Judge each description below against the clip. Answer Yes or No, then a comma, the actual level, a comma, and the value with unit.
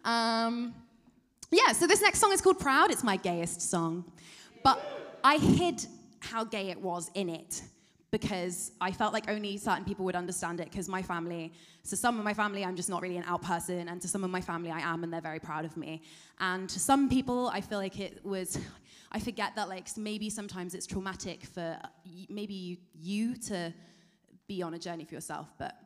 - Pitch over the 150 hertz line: Yes, medium, 185 Hz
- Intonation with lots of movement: No, average, 3.7 semitones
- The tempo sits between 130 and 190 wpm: No, fast, 205 wpm